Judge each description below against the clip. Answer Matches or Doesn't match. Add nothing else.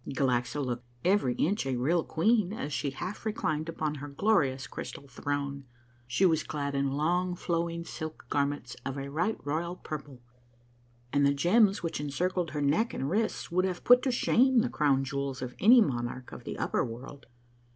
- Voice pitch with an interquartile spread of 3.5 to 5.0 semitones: Matches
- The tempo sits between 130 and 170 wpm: Doesn't match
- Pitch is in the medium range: Matches